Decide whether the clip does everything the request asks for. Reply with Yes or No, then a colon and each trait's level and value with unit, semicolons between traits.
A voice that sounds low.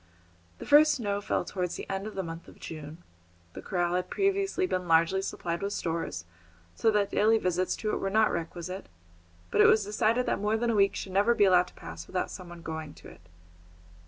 No: high, 190 Hz